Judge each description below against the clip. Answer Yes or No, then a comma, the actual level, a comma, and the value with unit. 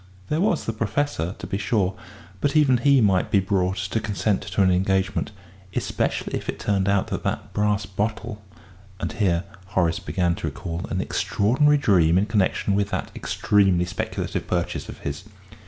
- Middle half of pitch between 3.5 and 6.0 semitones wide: No, average, 2.9 semitones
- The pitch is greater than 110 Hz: No, low, 100 Hz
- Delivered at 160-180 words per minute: Yes, average, 170 wpm